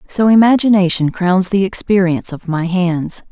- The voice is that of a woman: Yes, female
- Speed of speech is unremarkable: Yes, average, 145 wpm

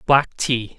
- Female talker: No, male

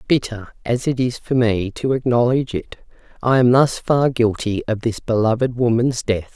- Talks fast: No, average, 180 wpm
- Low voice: Yes, low, 120 Hz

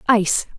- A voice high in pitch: Yes, high, 210 Hz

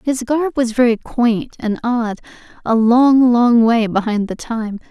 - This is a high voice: Yes, high, 235 Hz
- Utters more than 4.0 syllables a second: No, 3.9 syllables/s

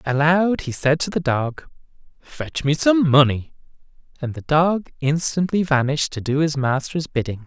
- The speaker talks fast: No, average, 160 wpm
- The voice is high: No, medium, 150 Hz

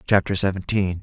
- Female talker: No, male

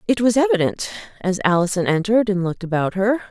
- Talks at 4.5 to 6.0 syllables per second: No, 6.6 syllables/s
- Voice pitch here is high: Yes, high, 205 Hz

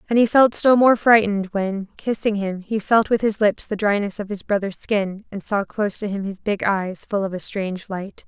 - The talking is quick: Yes, fast, 240 wpm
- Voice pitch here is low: No, high, 205 Hz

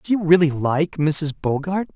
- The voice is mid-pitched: Yes, medium, 160 Hz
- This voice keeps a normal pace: Yes, average, 185 wpm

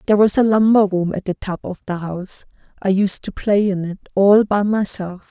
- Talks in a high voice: Yes, high, 195 Hz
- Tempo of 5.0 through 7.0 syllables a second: Yes, 5.3 syllables/s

